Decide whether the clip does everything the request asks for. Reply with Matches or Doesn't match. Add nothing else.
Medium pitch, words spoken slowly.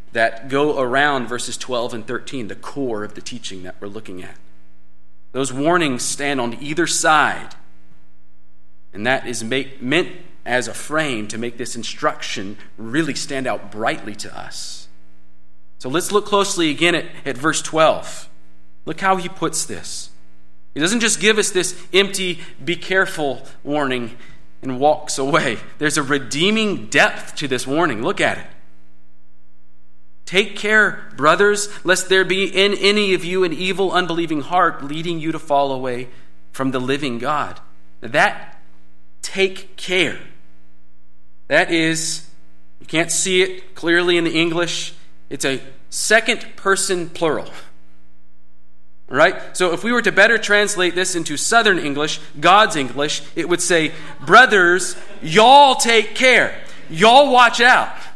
Doesn't match